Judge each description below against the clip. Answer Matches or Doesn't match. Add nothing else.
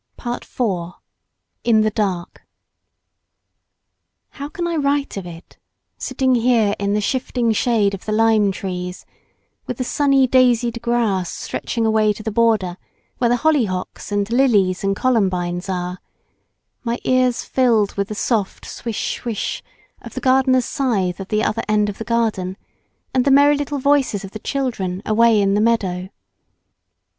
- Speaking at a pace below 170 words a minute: Matches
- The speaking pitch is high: Matches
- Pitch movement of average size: Matches